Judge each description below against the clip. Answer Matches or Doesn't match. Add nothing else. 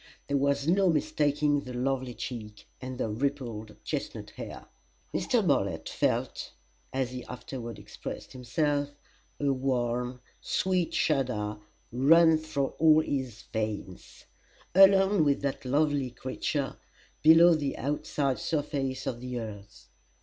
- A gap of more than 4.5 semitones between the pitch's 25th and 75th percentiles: Doesn't match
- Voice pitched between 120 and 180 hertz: Matches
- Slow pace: Matches